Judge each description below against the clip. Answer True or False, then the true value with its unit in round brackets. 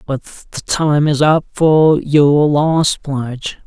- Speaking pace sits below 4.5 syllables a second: True (3.0 syllables/s)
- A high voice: False (145 Hz)